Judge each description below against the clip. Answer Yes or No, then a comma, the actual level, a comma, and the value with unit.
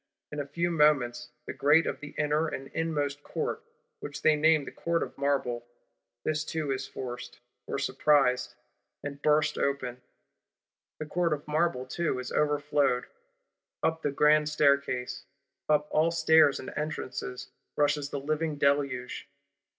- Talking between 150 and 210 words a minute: No, average, 140 wpm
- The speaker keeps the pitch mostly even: Yes, narrow, 2.0 semitones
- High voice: No, medium, 145 Hz